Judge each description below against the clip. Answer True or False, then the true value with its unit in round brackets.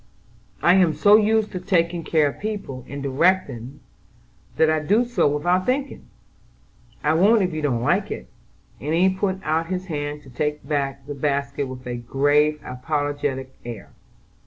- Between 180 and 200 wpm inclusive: False (165 wpm)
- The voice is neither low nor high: True (150 Hz)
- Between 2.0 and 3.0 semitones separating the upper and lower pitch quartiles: False (4.8 semitones)